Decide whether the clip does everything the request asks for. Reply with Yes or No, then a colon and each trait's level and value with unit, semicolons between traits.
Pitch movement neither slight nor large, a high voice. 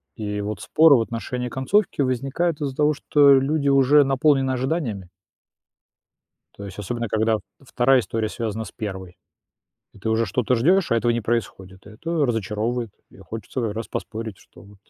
No: average, 4.1 semitones; low, 120 Hz